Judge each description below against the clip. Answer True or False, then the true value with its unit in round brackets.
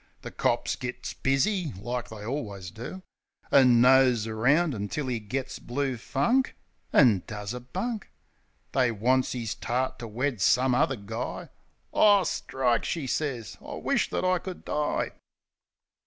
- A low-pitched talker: True (130 Hz)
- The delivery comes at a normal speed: True (145 wpm)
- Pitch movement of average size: True (4.0 semitones)